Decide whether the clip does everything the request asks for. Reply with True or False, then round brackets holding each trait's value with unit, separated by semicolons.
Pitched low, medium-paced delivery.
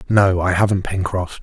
True (95 Hz; 170 wpm)